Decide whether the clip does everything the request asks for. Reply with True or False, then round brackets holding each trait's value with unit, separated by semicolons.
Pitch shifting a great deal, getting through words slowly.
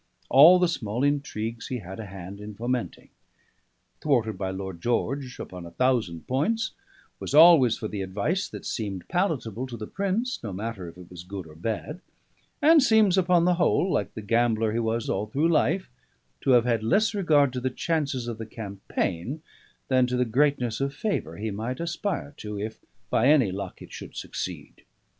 False (6.6 semitones; 185 wpm)